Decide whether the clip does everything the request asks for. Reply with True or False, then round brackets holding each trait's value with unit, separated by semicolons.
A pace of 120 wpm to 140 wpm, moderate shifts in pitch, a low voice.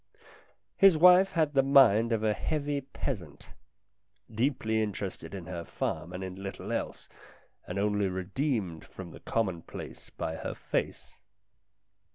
False (135 wpm; 6.9 semitones; 105 Hz)